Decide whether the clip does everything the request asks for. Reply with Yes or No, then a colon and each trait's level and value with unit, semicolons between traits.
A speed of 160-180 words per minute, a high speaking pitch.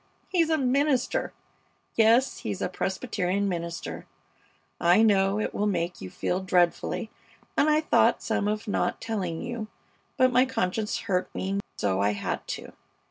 No: average, 150 wpm; high, 200 Hz